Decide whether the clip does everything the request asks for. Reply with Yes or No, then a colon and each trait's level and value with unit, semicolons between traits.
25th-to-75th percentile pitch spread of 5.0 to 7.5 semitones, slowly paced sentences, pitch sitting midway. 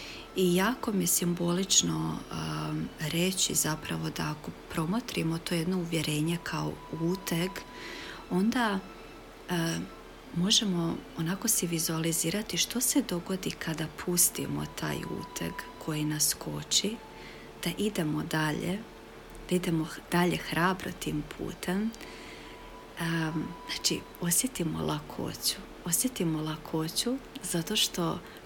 No: average, 3.2 semitones; slow, 105 wpm; medium, 170 Hz